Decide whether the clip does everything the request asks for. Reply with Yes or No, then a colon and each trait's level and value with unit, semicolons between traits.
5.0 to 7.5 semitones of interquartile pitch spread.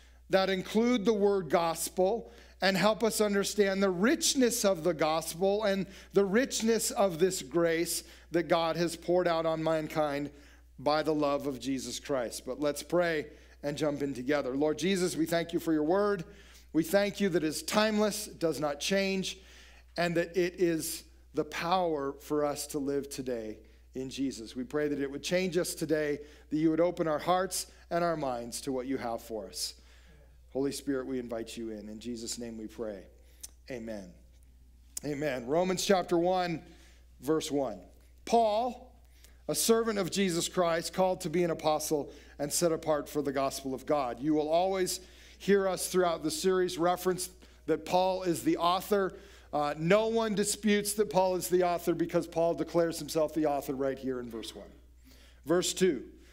Yes: average, 5.3 semitones